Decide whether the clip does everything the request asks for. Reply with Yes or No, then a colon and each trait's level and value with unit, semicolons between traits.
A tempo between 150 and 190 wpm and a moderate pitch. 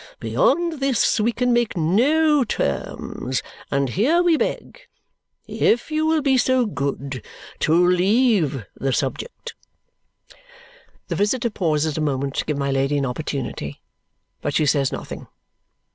No: slow, 135 wpm; medium, 180 Hz